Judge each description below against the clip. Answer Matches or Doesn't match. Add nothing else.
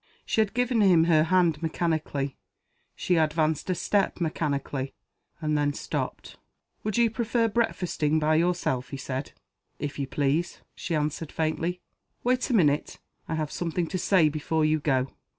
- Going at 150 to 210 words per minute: Matches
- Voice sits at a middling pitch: Matches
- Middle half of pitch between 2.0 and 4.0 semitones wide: Matches